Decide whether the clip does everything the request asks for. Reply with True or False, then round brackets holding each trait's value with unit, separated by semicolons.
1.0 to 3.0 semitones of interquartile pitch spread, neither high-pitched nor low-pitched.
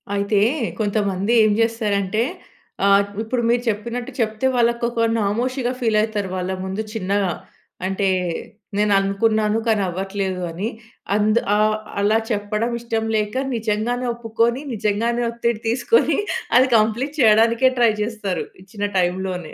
False (2.6 semitones; 215 Hz)